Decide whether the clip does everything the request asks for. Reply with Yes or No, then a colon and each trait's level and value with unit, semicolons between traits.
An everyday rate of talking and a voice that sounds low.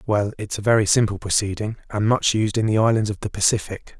No: fast, 225 wpm; low, 105 Hz